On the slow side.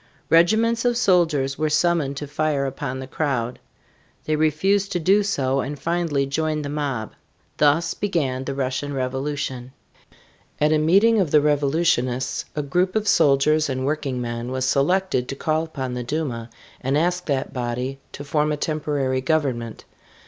No: average, 160 wpm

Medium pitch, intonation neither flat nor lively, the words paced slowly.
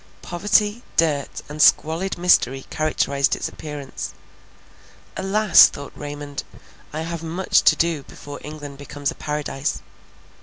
Yes: medium, 150 Hz; average, 3.0 semitones; slow, 120 wpm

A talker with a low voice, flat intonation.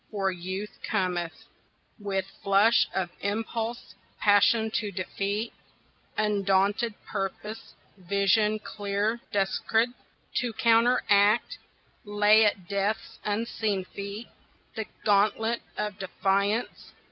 No: high, 205 Hz; narrow, 1.9 semitones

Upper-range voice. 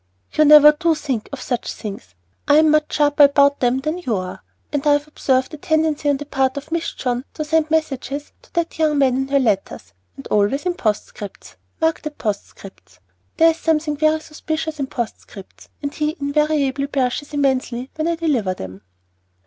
Yes: very high, 290 Hz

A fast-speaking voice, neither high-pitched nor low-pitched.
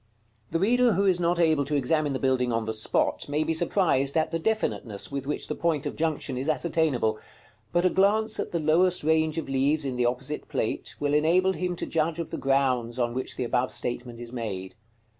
Yes: fast, 230 wpm; medium, 150 Hz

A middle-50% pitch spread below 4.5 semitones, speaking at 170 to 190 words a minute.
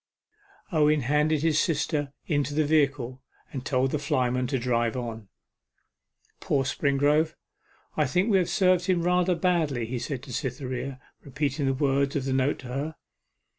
No: average, 3.2 semitones; average, 160 wpm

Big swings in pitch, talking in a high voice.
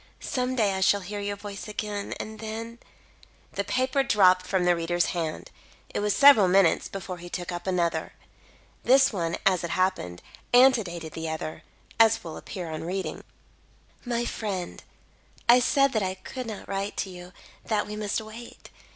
No: average, 4.0 semitones; high, 200 Hz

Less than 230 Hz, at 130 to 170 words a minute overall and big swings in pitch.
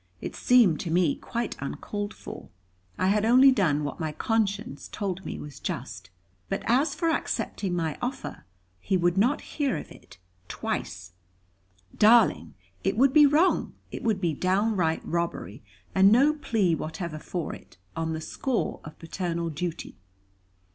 Yes: high, 190 Hz; average, 155 wpm; wide, 6.4 semitones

